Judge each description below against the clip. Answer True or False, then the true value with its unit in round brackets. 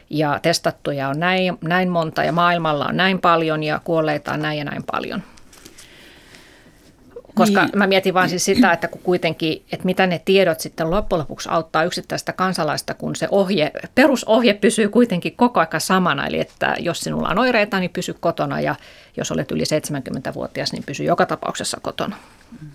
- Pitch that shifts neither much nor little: True (3.0 semitones)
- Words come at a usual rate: False (170 wpm)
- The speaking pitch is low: False (175 Hz)